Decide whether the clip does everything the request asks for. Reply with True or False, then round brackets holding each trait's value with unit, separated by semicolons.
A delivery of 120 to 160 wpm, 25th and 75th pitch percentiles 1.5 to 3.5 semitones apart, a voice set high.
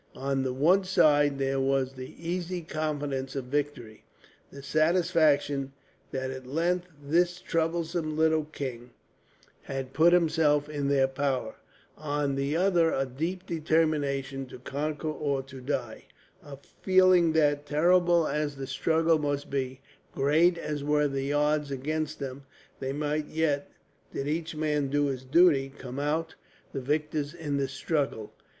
False (145 wpm; 2.8 semitones; 145 Hz)